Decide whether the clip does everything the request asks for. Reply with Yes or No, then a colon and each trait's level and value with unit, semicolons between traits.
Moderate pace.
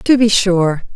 Yes: average, 190 wpm